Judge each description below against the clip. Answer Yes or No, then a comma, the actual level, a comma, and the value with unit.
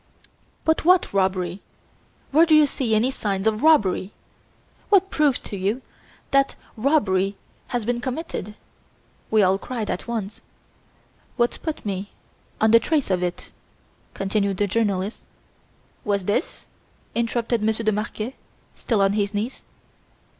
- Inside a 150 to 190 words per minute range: No, average, 140 wpm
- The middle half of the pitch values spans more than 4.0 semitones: Yes, average, 4.5 semitones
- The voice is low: No, high, 215 Hz